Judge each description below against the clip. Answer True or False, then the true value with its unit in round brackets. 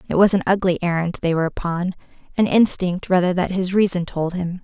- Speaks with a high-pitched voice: False (180 Hz)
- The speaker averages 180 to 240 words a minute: True (205 wpm)